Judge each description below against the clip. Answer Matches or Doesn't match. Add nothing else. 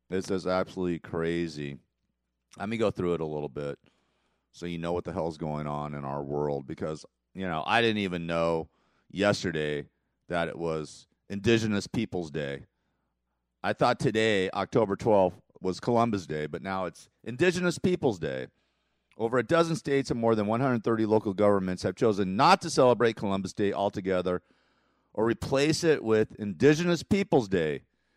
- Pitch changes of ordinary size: Doesn't match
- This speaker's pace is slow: Doesn't match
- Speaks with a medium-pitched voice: Doesn't match